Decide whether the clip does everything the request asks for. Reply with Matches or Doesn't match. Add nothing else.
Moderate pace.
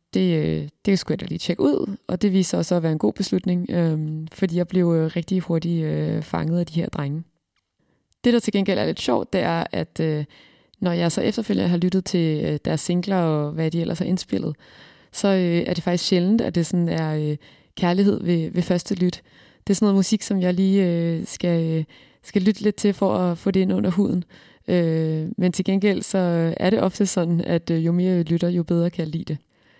Doesn't match